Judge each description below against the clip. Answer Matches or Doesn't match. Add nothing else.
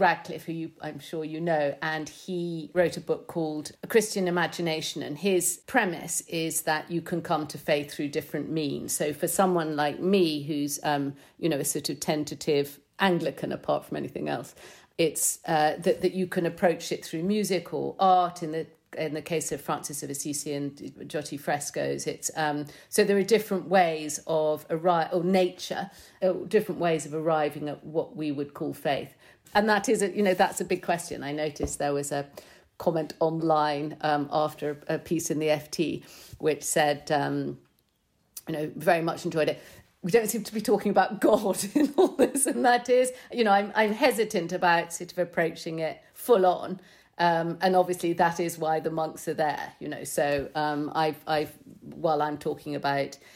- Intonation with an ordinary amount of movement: Matches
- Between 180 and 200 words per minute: Matches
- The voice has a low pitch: Doesn't match